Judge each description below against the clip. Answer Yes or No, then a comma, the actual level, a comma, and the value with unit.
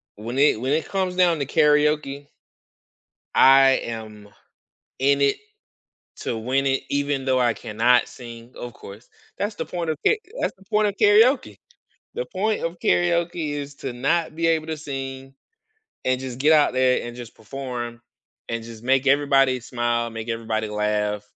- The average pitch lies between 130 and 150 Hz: Yes, low, 135 Hz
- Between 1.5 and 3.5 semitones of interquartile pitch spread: No, average, 4.5 semitones